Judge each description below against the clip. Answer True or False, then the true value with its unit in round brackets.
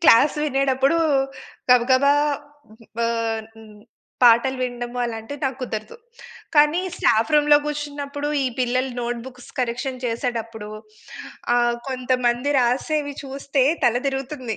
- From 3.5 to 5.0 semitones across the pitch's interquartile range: False (2.8 semitones)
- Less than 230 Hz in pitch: False (250 Hz)